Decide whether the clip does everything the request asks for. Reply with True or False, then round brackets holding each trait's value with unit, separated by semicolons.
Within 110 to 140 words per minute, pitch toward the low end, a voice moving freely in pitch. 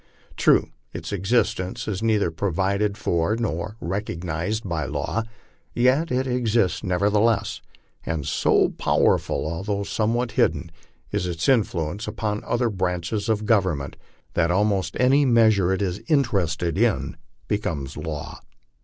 False (135 wpm; 100 Hz; 4.5 semitones)